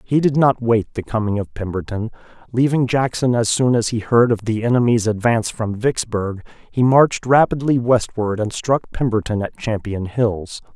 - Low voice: Yes, low, 115 Hz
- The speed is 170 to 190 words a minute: Yes, average, 175 wpm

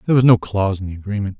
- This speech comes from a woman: No, male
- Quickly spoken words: Yes, fast, 300 wpm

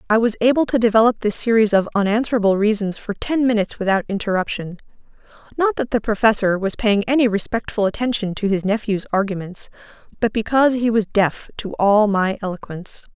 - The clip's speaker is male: No, female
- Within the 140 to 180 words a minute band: Yes, average, 170 wpm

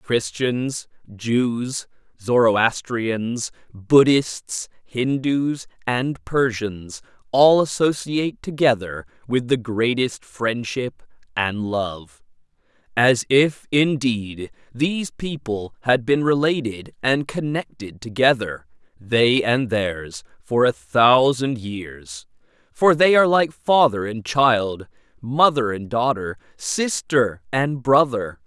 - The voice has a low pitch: Yes, low, 120 Hz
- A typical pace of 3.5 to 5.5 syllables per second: No, 3.2 syllables/s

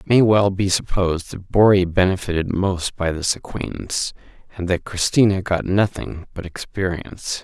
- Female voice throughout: No, male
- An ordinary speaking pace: Yes, average, 155 wpm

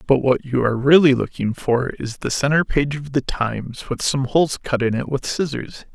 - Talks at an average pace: No, fast, 220 wpm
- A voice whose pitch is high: No, low, 135 Hz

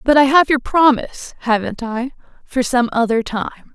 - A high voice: Yes, very high, 250 Hz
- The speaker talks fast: No, average, 145 wpm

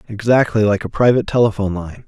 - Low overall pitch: Yes, low, 105 Hz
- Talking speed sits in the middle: Yes, average, 175 wpm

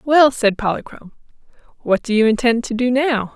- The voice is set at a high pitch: Yes, high, 235 Hz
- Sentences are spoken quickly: No, average, 180 wpm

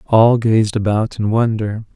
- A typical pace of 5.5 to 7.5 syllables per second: No, 4.1 syllables/s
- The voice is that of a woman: No, male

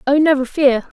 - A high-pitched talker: Yes, very high, 275 Hz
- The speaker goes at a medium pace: Yes, average, 180 wpm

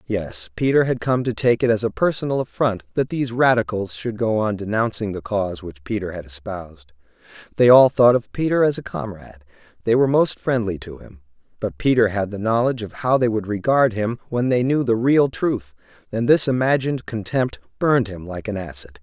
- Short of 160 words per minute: No, average, 200 wpm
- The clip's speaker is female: No, male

